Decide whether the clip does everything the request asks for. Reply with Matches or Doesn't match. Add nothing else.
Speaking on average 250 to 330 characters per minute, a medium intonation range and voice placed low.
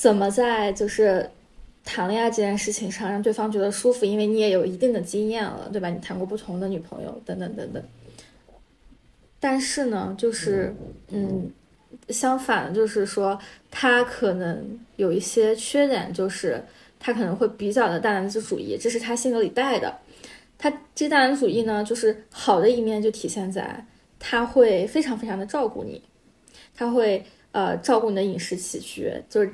Doesn't match